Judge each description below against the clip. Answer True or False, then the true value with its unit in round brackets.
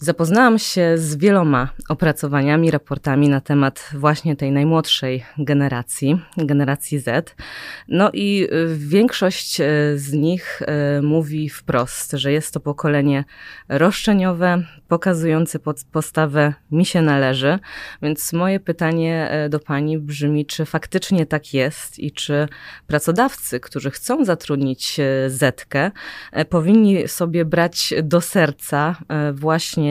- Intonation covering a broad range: False (2.7 semitones)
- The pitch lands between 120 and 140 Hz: False (155 Hz)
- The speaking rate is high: False (110 wpm)